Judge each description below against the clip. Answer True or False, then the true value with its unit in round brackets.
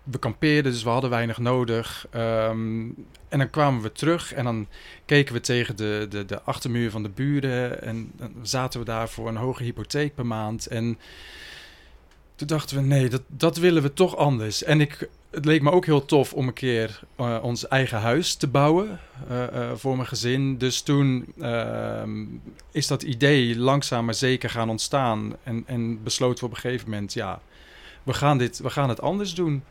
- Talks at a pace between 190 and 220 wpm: True (195 wpm)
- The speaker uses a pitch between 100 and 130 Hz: True (125 Hz)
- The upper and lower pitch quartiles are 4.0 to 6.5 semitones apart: False (3.6 semitones)